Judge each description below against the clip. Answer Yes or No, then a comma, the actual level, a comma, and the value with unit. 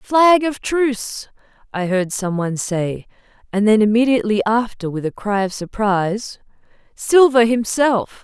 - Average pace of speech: No, slow, 130 wpm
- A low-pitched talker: No, high, 220 Hz